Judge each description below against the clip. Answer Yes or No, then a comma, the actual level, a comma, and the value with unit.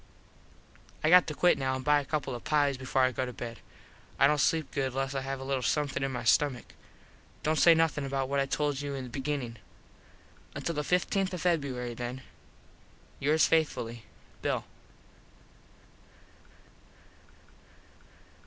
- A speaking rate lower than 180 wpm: Yes, average, 155 wpm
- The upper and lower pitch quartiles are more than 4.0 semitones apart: No, narrow, 2.5 semitones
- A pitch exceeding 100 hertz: Yes, medium, 140 Hz